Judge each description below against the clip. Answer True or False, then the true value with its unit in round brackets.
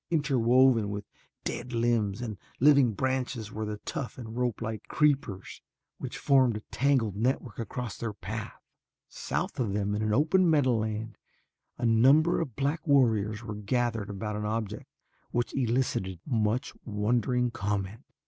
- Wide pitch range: False (3.7 semitones)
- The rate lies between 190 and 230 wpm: False (140 wpm)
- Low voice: True (115 Hz)